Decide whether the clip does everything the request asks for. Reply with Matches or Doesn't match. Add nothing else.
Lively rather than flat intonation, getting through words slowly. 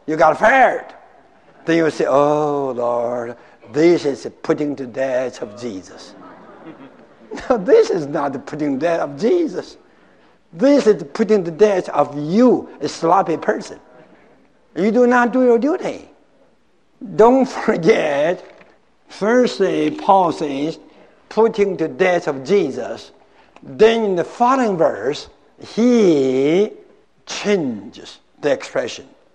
Matches